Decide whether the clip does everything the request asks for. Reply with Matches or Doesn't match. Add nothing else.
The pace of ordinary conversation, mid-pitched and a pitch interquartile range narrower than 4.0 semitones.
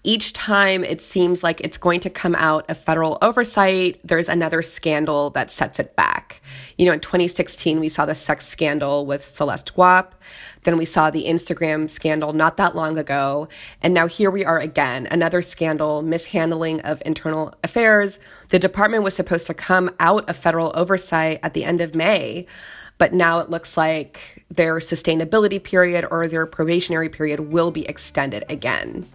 Matches